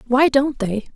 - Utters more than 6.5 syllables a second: No, 4.4 syllables/s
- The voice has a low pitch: No, very high, 255 Hz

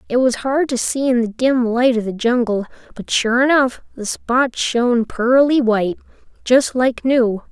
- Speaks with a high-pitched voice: Yes, high, 245 Hz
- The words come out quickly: No, average, 185 wpm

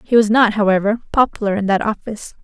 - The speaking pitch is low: No, high, 215 Hz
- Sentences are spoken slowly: No, average, 200 wpm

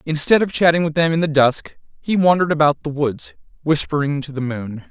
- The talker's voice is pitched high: No, medium, 150 Hz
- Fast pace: Yes, fast, 210 wpm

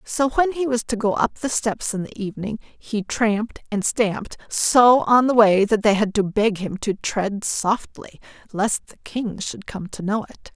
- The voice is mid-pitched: No, high, 215 Hz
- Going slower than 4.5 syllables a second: Yes, 4.2 syllables/s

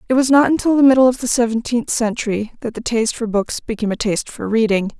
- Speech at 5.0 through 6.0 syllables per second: No, 6.6 syllables/s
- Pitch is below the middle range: No, high, 235 Hz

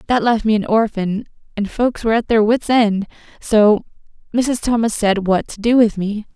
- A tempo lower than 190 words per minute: No, average, 200 wpm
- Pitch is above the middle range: Yes, high, 220 Hz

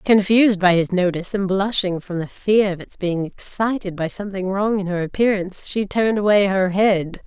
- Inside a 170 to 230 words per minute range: Yes, average, 200 wpm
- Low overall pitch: No, high, 195 Hz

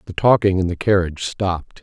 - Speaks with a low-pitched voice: Yes, very low, 95 Hz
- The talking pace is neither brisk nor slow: Yes, average, 195 wpm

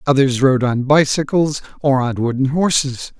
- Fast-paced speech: No, average, 150 wpm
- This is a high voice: No, low, 135 Hz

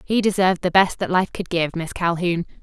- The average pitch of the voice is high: No, medium, 180 Hz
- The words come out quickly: Yes, fast, 230 wpm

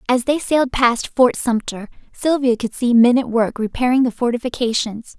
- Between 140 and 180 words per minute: Yes, average, 175 wpm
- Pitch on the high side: Yes, high, 245 Hz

